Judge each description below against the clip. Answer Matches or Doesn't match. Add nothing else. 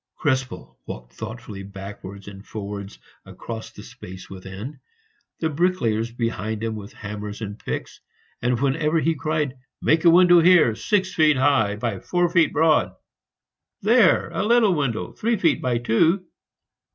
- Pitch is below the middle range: Matches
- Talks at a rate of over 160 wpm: Doesn't match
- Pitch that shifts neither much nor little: Doesn't match